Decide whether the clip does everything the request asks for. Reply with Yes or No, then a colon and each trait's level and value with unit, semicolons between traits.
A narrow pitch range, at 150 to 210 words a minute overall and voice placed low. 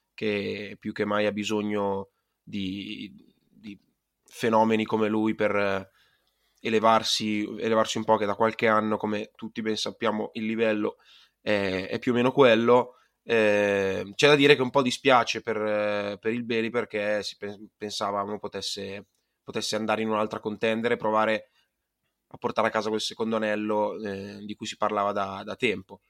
Yes: narrow, 1.3 semitones; average, 165 wpm; low, 105 Hz